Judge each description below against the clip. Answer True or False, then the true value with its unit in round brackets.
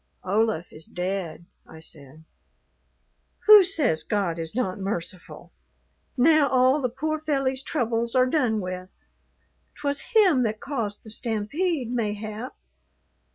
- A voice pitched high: True (230 Hz)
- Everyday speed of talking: False (120 wpm)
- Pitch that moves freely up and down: True (6.4 semitones)